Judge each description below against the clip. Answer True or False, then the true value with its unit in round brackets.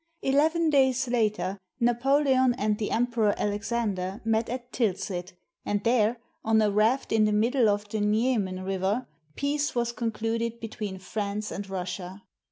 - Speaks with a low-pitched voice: False (220 Hz)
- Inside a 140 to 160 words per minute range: True (150 wpm)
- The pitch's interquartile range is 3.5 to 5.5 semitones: False (3.1 semitones)